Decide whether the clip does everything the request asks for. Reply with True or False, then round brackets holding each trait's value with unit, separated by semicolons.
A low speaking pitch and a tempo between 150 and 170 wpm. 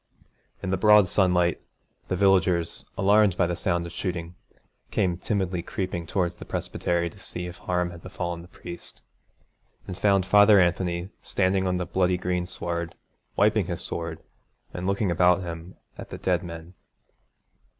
True (90 Hz; 160 wpm)